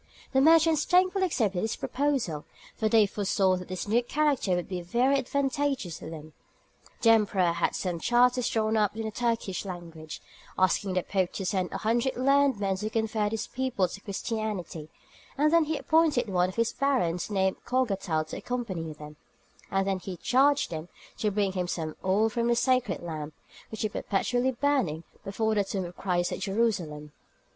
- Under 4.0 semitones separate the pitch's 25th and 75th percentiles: No, wide, 5.4 semitones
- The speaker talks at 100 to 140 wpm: No, average, 175 wpm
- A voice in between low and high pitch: No, high, 210 Hz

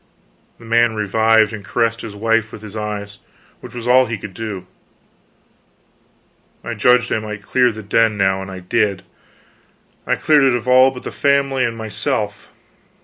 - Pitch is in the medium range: No, low, 110 Hz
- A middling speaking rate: Yes, average, 165 wpm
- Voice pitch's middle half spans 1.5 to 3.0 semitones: Yes, average, 2.7 semitones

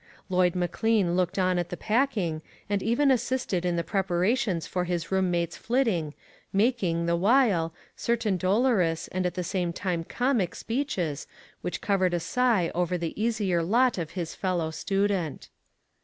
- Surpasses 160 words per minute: No, average, 155 wpm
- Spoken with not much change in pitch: No, average, 4.4 semitones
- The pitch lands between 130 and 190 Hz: Yes, medium, 185 Hz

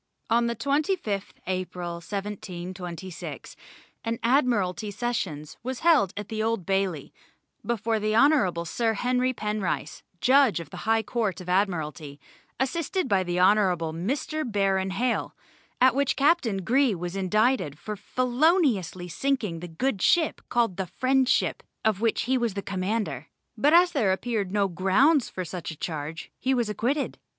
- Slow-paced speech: No, average, 145 wpm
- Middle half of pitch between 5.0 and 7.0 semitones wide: Yes, wide, 5.5 semitones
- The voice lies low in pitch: No, high, 210 Hz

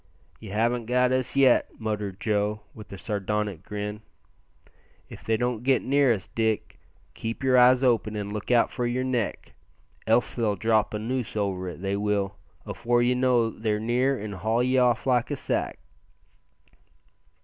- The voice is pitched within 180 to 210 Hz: No, low, 115 Hz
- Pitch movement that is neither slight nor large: Yes, average, 3.0 semitones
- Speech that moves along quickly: No, average, 165 wpm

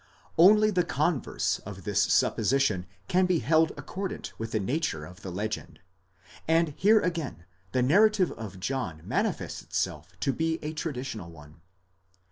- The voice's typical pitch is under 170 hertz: Yes, low, 135 Hz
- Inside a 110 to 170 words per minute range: Yes, average, 150 wpm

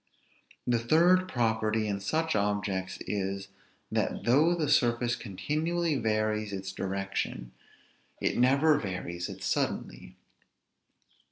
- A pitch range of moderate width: No, wide, 6.9 semitones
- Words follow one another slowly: Yes, slow, 105 wpm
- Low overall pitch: Yes, low, 110 Hz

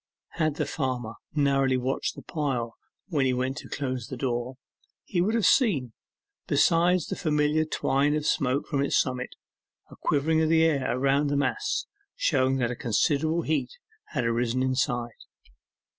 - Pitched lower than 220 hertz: Yes, medium, 140 Hz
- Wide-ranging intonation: No, average, 3.5 semitones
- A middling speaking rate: Yes, average, 160 wpm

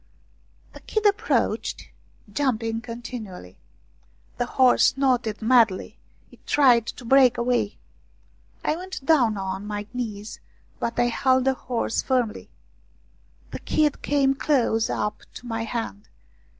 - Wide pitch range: No, average, 3.2 semitones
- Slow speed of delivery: Yes, slow, 125 wpm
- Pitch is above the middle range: Yes, high, 240 Hz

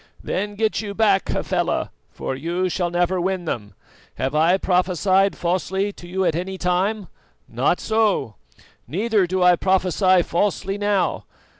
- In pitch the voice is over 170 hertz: Yes, medium, 185 Hz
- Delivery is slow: No, average, 145 wpm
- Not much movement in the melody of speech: Yes, narrow, 2.2 semitones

